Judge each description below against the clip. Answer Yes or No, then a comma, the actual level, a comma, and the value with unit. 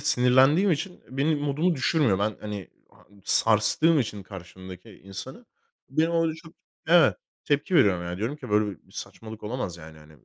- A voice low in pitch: Yes, low, 125 Hz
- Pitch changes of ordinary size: No, wide, 7.9 semitones